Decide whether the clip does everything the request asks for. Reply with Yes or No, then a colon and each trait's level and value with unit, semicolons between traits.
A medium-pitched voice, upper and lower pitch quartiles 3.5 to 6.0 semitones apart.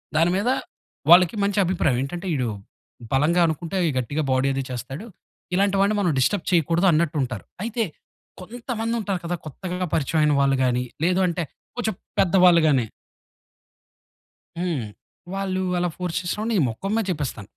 Yes: medium, 175 Hz; average, 5.1 semitones